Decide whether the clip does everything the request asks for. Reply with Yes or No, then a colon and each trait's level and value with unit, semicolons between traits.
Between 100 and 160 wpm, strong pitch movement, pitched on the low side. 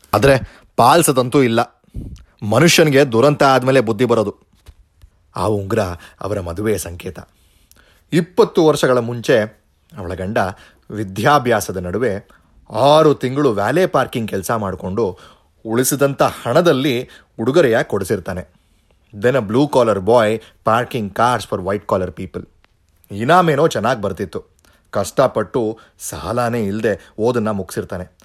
Yes: fast, 105 wpm; wide, 5.8 semitones; low, 110 Hz